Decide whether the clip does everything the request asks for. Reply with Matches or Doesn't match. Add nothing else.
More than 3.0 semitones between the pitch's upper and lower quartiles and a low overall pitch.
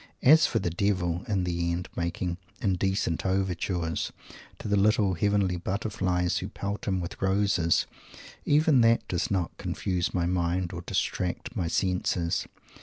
Doesn't match